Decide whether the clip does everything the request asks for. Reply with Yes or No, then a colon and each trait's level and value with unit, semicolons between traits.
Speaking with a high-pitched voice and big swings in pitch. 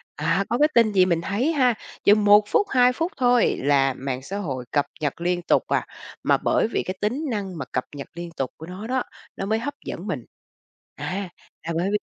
Yes: high, 195 Hz; wide, 6.1 semitones